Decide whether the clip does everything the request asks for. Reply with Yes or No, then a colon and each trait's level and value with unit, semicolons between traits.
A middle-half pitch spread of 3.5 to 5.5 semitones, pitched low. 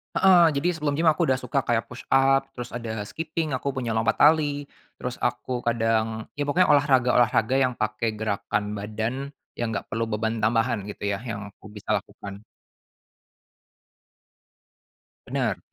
Yes: average, 4.3 semitones; low, 120 Hz